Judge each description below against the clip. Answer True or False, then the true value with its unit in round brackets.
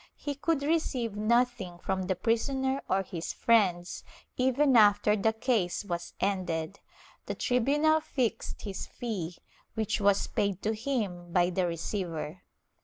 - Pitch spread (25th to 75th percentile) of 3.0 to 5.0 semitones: False (5.4 semitones)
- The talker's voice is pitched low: False (210 Hz)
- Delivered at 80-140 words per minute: True (135 wpm)